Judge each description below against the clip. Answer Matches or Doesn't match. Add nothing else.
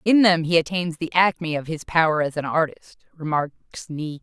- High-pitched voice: Doesn't match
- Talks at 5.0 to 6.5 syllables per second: Doesn't match